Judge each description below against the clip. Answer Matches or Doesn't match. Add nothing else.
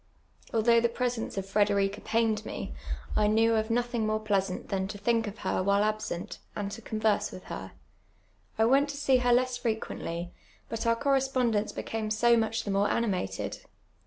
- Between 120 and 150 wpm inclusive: Doesn't match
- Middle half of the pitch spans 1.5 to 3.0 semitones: Matches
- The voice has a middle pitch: Doesn't match